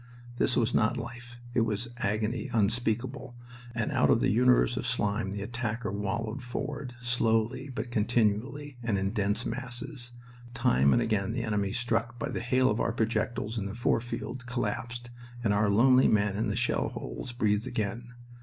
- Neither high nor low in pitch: No, low, 115 Hz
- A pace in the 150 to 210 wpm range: Yes, average, 175 wpm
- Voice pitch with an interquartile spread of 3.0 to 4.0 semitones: No, narrow, 2.6 semitones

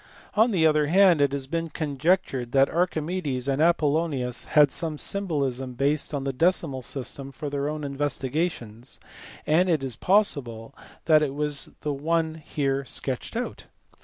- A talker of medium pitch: Yes, medium, 145 Hz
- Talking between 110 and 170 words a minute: Yes, average, 155 wpm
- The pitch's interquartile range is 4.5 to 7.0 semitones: No, average, 3.3 semitones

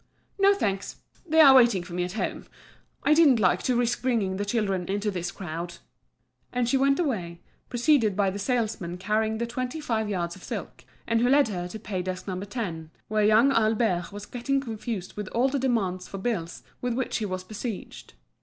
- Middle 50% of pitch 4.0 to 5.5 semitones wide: Yes, average, 4.7 semitones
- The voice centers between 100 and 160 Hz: No, high, 215 Hz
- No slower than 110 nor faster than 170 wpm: No, average, 200 wpm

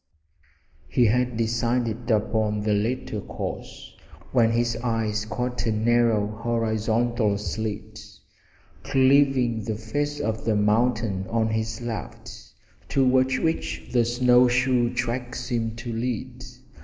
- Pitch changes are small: Yes, narrow, 2.0 semitones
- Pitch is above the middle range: No, low, 115 Hz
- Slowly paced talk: Yes, slow, 120 wpm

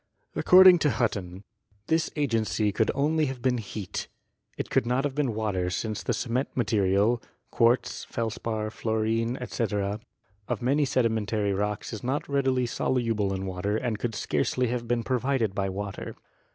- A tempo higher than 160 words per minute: Yes, average, 170 wpm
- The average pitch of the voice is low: Yes, low, 115 Hz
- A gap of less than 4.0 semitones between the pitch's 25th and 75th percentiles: Yes, average, 3.6 semitones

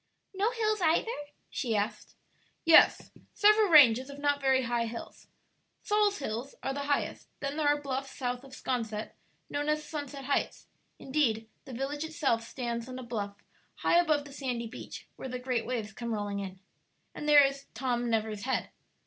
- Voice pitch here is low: No, very high, 265 Hz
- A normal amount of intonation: Yes, average, 3.9 semitones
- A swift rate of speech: No, average, 175 wpm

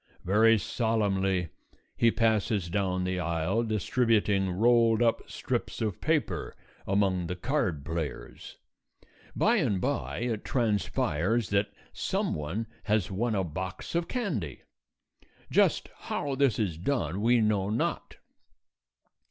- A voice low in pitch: Yes, low, 105 Hz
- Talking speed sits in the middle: No, slow, 120 wpm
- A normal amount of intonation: Yes, average, 4.1 semitones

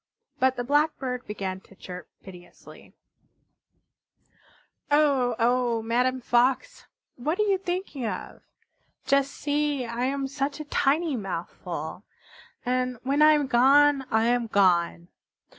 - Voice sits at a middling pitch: No, very high, 255 Hz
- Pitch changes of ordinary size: Yes, average, 3.9 semitones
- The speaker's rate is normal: No, slow, 125 wpm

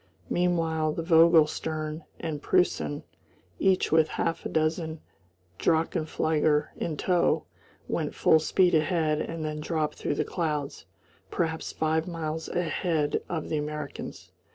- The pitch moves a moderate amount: No, narrow, 1.5 semitones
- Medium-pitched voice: Yes, medium, 160 Hz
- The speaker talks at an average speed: No, slow, 130 wpm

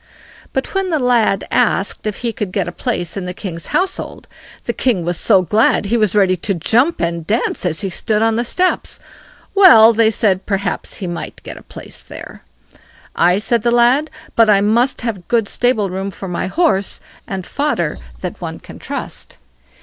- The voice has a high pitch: Yes, high, 210 Hz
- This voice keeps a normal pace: Yes, average, 190 wpm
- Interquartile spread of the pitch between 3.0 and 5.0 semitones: Yes, average, 4.2 semitones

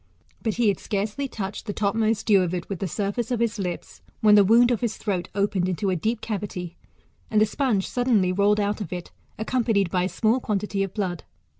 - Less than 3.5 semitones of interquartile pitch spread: Yes, narrow, 2.6 semitones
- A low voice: No, high, 205 Hz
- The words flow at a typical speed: No, fast, 215 wpm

